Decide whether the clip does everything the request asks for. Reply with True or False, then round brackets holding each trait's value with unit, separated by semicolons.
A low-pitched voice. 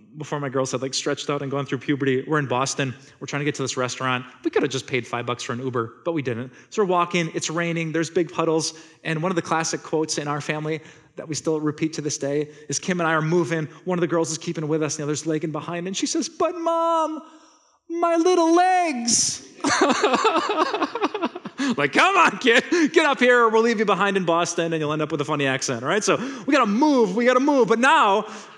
False (160 Hz)